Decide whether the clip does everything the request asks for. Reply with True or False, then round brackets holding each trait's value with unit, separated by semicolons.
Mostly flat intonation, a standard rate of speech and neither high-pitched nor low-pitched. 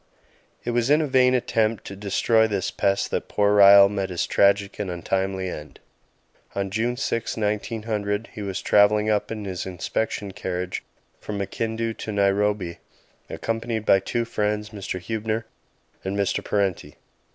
False (2.3 semitones; 150 wpm; 105 Hz)